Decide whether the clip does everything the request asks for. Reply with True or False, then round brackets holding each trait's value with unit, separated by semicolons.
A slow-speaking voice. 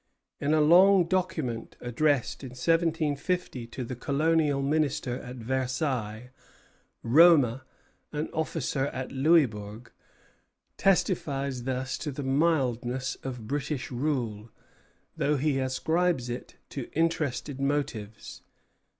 True (105 wpm)